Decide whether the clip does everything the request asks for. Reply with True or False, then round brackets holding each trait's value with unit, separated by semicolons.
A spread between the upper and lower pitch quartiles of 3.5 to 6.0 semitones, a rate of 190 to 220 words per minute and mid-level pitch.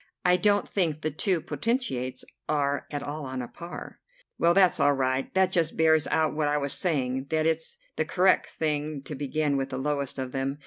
False (3.1 semitones; 205 wpm; 150 Hz)